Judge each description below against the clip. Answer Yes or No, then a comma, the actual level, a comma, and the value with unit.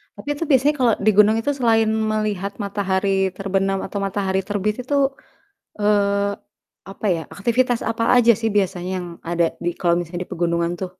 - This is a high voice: Yes, high, 200 Hz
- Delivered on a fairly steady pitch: No, average, 3.0 semitones